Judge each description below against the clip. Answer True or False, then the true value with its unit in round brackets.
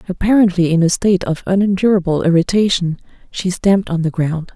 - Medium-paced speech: True (160 wpm)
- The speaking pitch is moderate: True (180 Hz)